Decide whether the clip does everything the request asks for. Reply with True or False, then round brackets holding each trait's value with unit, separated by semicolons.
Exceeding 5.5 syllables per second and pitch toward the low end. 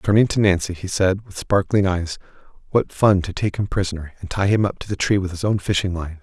True (5.7 syllables/s; 95 Hz)